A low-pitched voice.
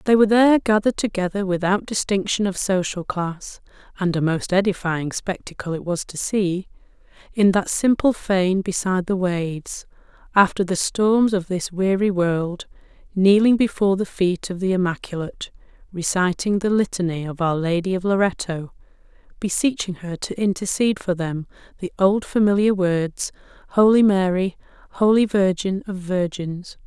No: high, 190 Hz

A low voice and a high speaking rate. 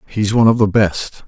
Yes: low, 105 Hz; fast, 235 wpm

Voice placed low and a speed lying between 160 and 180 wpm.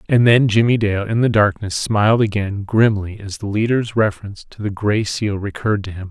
No: low, 105 Hz; fast, 205 wpm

